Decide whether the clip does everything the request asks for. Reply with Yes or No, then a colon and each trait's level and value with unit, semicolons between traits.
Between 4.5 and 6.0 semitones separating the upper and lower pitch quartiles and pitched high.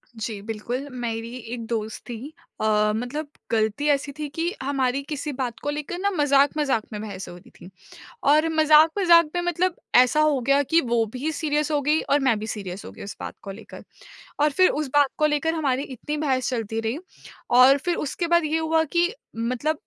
Yes: average, 4.9 semitones; very high, 280 Hz